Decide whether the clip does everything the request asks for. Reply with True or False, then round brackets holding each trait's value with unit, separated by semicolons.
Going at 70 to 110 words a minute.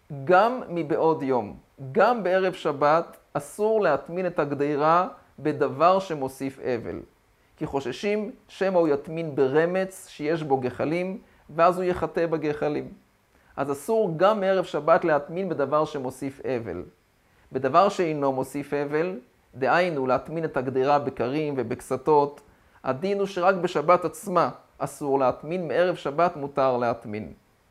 False (120 wpm)